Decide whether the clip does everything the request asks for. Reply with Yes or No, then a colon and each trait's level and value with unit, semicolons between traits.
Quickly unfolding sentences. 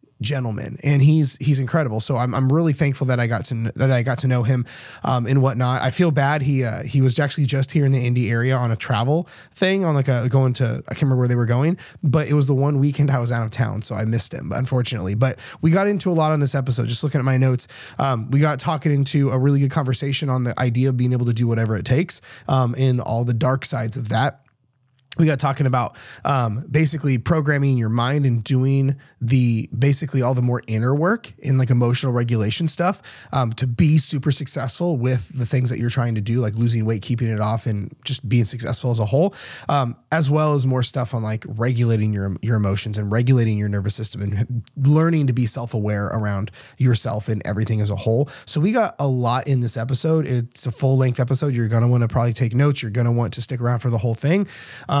Yes: fast, 240 wpm